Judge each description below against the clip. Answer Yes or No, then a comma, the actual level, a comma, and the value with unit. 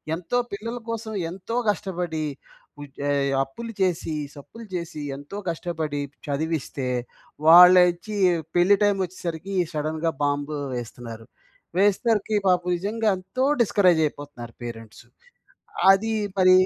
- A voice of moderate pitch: Yes, medium, 175 Hz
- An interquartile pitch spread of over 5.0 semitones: Yes, wide, 5.4 semitones